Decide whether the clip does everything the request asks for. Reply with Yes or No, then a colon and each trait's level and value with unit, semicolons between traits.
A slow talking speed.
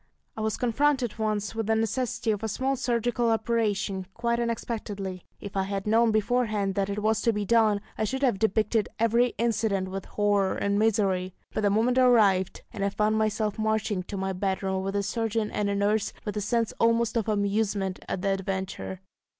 No: average, 190 wpm